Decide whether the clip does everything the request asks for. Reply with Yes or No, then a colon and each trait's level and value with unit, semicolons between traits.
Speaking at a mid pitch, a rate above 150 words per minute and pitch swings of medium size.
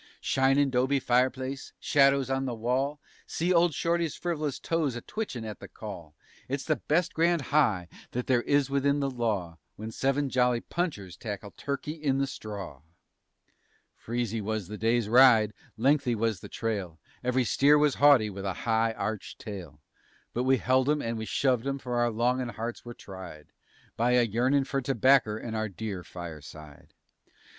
No: low, 125 Hz; average, 170 wpm; average, 4.1 semitones